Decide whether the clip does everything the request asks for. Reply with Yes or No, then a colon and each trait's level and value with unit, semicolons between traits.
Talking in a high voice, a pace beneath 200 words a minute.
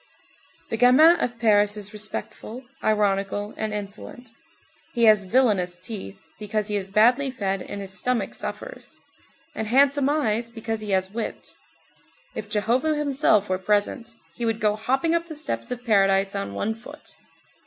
Yes: high, 215 Hz; average, 155 wpm